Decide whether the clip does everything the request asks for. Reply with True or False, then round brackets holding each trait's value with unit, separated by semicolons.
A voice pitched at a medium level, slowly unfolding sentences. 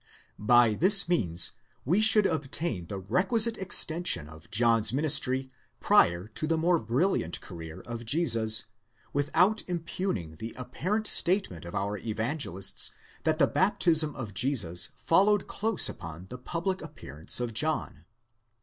False (130 Hz; 130 wpm)